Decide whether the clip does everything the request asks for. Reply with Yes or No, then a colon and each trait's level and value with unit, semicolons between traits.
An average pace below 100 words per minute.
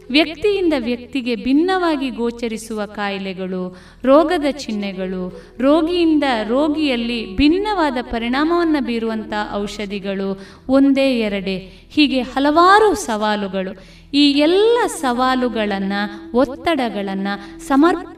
Yes: average, 75 wpm